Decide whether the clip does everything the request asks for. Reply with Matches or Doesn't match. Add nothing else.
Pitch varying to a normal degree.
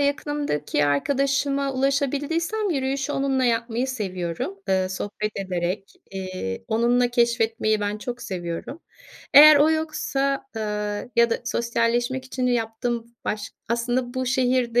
Matches